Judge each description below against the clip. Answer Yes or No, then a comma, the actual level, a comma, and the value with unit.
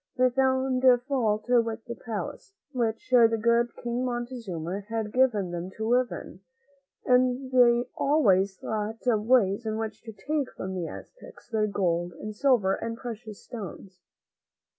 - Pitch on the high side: Yes, high, 230 Hz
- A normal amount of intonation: Yes, average, 3.3 semitones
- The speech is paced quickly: No, average, 150 wpm